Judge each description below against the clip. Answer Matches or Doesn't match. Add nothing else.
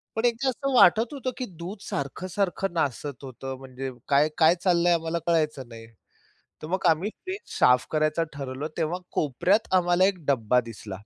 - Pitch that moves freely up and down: Matches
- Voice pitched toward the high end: Doesn't match